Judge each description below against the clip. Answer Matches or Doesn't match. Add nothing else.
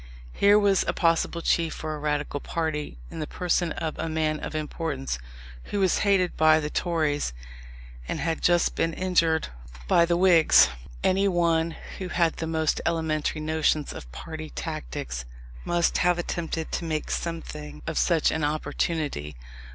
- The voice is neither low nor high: Matches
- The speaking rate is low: Doesn't match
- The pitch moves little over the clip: Matches